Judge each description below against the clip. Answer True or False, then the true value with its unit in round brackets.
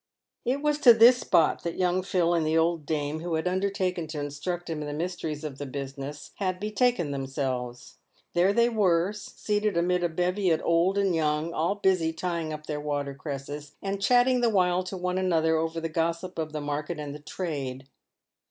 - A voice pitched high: False (170 Hz)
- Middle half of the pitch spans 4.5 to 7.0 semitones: False (3.8 semitones)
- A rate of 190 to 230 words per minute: True (200 wpm)